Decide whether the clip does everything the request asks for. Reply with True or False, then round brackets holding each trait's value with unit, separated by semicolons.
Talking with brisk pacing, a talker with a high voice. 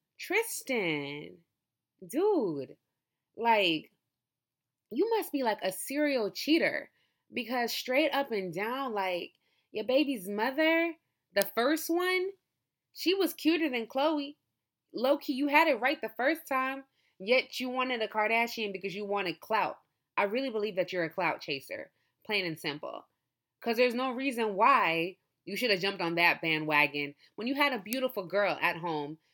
False (155 wpm; 230 Hz)